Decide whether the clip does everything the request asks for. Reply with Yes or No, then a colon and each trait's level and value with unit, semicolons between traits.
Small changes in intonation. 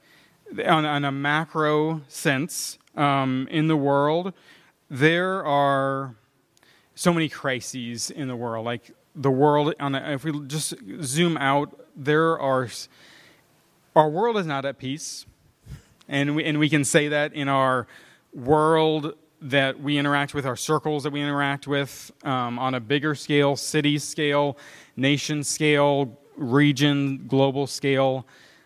Yes: narrow, 2.0 semitones